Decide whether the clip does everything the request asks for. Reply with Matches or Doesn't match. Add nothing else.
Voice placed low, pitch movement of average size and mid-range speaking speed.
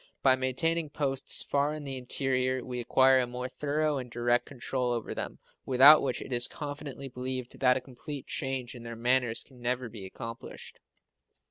Doesn't match